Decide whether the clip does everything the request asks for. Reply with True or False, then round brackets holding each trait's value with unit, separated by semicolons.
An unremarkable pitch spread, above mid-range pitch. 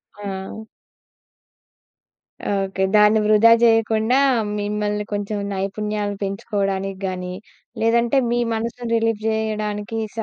False (2.0 semitones; 210 Hz)